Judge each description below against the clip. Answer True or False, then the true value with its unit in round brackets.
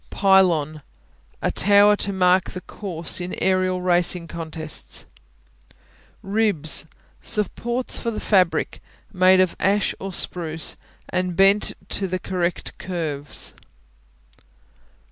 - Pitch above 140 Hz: True (185 Hz)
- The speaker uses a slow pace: True (105 wpm)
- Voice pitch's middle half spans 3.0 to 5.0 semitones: False (2.5 semitones)